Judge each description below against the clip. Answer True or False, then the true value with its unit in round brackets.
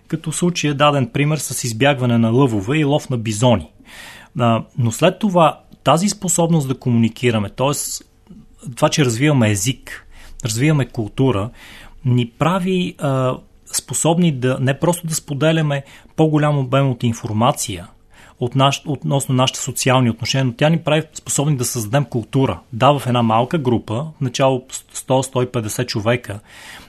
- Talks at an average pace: True (140 wpm)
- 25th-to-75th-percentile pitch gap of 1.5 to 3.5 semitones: False (4.0 semitones)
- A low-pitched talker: True (130 Hz)